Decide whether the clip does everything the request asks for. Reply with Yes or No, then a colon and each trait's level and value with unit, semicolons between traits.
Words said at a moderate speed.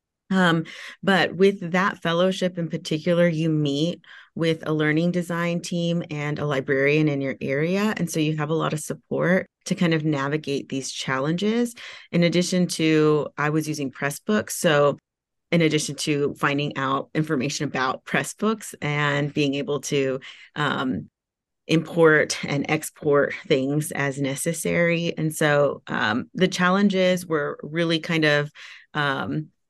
Yes: average, 145 wpm